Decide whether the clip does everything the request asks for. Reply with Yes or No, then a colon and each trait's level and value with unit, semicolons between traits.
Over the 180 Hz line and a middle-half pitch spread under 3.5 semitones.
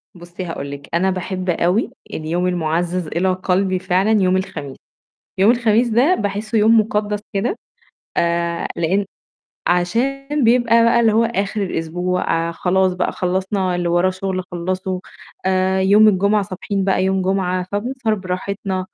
Yes: high, 190 Hz; average, 2.8 semitones